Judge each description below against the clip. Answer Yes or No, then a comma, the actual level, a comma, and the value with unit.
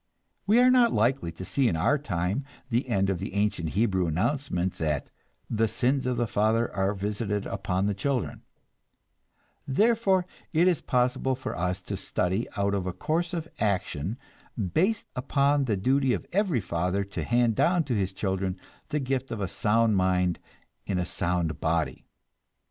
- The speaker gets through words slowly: No, average, 165 wpm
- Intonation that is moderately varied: No, wide, 6.3 semitones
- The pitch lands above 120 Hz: No, low, 105 Hz